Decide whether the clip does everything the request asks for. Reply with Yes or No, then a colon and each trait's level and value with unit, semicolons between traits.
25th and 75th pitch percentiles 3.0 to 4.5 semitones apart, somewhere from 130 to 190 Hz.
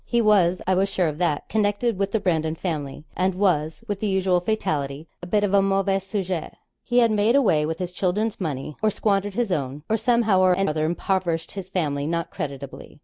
Yes: average, 4.2 semitones; medium, 185 Hz